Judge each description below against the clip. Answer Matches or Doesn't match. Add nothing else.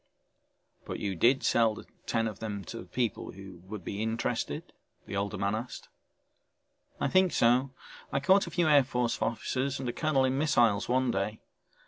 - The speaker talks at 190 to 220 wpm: Doesn't match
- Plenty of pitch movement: Doesn't match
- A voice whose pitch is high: Doesn't match